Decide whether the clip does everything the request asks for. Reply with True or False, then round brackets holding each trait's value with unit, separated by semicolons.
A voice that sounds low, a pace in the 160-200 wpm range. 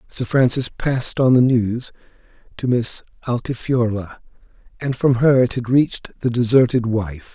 False (120 Hz; 145 wpm)